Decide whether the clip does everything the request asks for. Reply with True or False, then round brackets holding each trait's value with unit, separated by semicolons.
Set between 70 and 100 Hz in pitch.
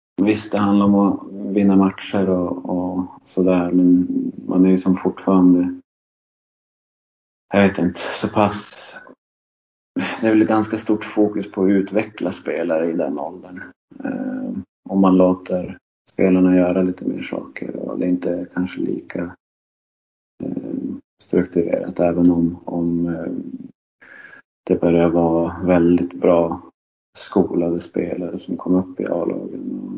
True (90 Hz)